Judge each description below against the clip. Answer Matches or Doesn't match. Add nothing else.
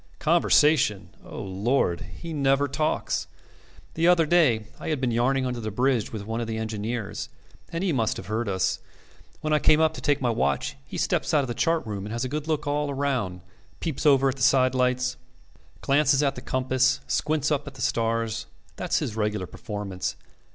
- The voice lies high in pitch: Doesn't match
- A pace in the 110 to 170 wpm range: Doesn't match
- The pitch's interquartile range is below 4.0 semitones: Doesn't match